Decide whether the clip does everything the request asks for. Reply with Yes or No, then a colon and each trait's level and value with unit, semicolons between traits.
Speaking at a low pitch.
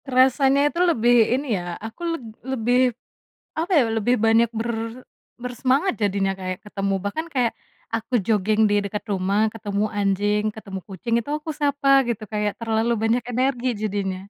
No: high, 225 Hz